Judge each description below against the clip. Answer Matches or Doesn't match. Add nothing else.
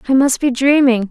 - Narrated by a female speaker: Matches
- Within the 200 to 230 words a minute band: Matches